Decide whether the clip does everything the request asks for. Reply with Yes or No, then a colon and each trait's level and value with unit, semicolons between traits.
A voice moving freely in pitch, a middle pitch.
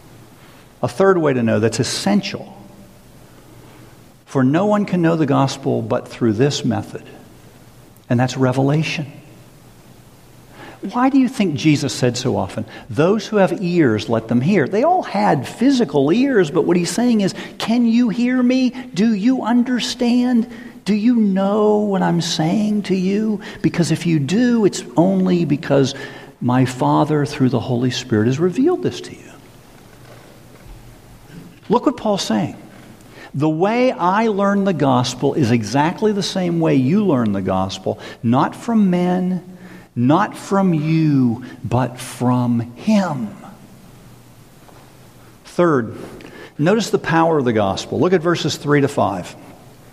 Yes: wide, 8.0 semitones; medium, 170 Hz